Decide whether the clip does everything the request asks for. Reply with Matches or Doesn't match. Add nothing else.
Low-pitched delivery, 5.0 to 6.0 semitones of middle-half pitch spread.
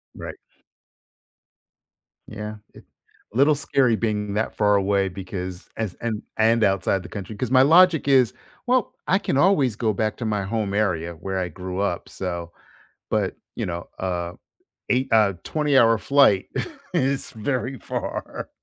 Matches